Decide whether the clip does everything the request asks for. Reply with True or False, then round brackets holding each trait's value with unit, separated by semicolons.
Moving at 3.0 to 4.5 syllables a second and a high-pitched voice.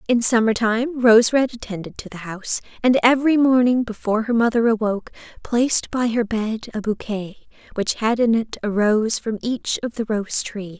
False (5.1 syllables/s; 225 Hz)